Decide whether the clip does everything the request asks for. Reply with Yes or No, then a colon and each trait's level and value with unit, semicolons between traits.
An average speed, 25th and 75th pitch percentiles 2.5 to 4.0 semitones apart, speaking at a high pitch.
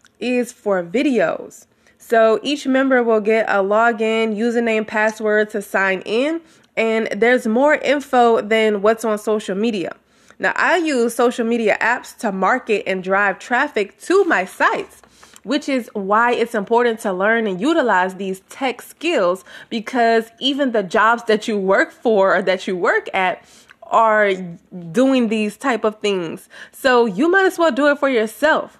Yes: average, 165 wpm; average, 3.4 semitones; high, 225 Hz